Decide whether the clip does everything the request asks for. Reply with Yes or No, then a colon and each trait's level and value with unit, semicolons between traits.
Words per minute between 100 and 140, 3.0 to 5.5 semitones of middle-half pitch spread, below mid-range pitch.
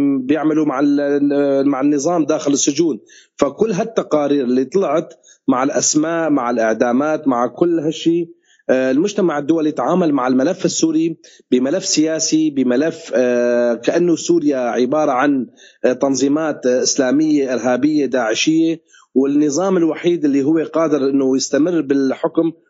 No: average, 110 wpm; average, 3.5 semitones; medium, 150 Hz